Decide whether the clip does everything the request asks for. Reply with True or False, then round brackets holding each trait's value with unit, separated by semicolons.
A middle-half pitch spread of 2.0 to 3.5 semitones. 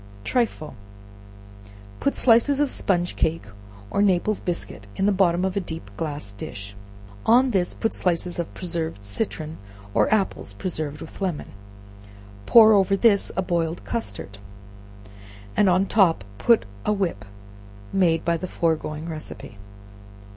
False (3.9 semitones)